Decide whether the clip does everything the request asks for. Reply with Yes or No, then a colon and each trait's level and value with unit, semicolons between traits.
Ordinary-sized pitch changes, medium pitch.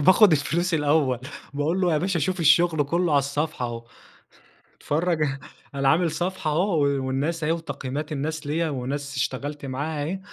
Yes: average, 3.1 semitones; medium, 150 Hz